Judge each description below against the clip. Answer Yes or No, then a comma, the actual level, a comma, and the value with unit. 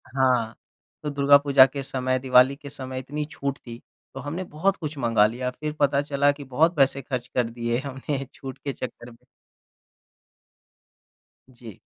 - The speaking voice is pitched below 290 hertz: Yes, low, 135 Hz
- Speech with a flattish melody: Yes, narrow, 2.1 semitones